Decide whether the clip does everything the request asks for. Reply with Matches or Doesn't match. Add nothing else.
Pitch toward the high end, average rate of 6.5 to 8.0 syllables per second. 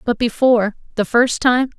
Doesn't match